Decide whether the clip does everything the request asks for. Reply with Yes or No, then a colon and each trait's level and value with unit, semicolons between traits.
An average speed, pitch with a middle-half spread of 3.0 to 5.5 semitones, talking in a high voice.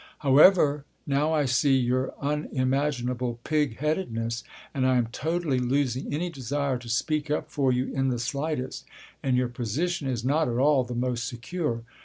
No: average, 170 wpm; average, 3.3 semitones; low, 135 Hz